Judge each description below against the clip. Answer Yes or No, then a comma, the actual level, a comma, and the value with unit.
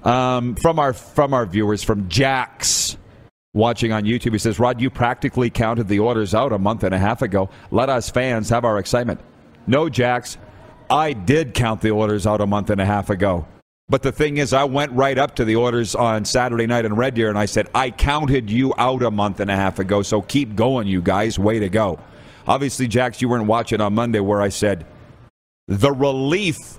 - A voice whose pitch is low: Yes, low, 115 Hz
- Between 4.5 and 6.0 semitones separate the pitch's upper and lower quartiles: No, average, 3.5 semitones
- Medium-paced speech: No, fast, 215 wpm